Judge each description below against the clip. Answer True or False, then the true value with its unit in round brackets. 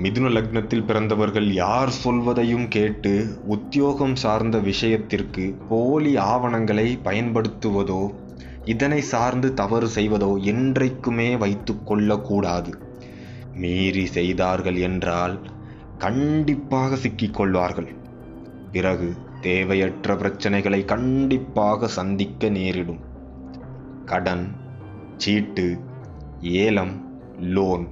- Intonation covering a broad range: False (4.3 semitones)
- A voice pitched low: True (105 Hz)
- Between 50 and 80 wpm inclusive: True (75 wpm)